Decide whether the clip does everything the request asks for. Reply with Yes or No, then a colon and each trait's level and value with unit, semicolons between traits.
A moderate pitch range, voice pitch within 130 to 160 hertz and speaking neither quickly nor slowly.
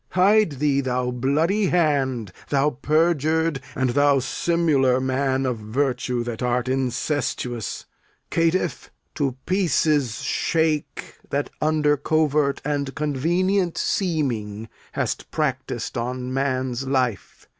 No: average, 3.6 semitones; medium, 140 Hz; slow, 105 wpm